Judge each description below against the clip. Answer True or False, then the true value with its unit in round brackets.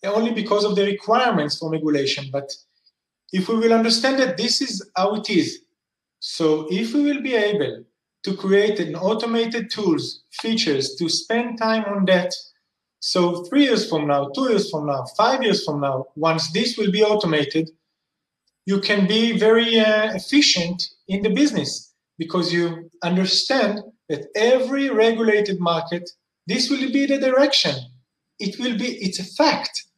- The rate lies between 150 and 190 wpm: True (160 wpm)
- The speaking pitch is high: True (205 Hz)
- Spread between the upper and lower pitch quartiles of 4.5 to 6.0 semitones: True (5.1 semitones)